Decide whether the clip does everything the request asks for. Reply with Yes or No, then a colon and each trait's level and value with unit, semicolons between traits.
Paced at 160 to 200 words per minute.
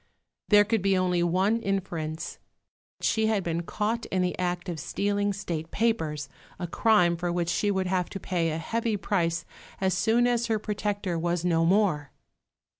Yes: average, 175 wpm